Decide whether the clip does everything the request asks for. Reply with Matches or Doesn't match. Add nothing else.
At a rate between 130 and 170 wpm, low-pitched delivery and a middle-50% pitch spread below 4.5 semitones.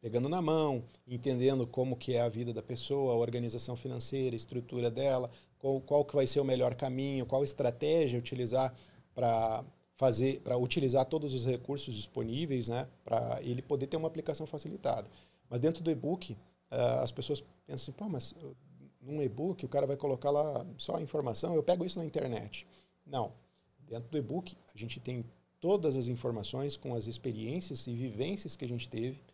Doesn't match